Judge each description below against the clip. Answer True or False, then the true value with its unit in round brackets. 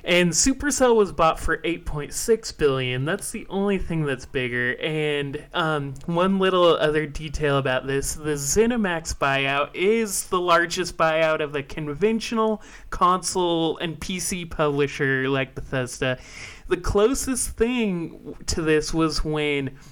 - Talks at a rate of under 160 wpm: True (135 wpm)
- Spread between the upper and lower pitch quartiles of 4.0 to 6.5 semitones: True (4.9 semitones)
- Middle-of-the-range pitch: True (160 Hz)